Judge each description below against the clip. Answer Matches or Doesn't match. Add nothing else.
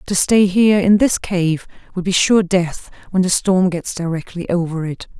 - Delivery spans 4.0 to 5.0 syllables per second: Matches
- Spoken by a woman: Matches